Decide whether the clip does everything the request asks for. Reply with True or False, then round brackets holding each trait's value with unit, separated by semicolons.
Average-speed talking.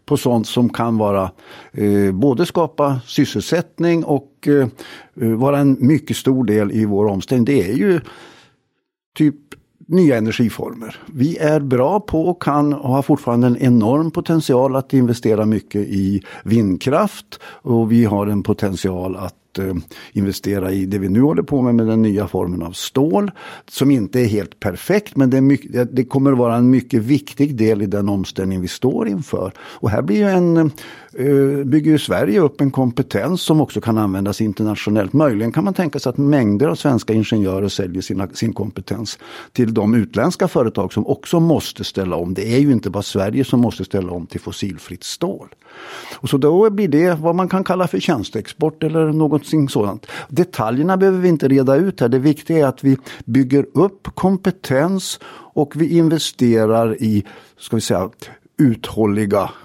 True (175 wpm)